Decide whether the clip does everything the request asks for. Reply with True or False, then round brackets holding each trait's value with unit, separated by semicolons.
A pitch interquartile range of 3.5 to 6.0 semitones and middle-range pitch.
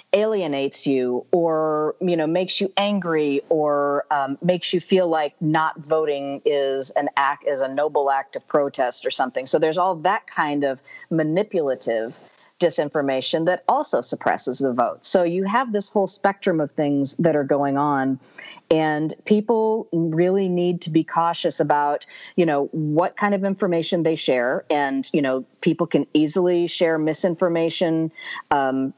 True (3.9 semitones; 160 Hz)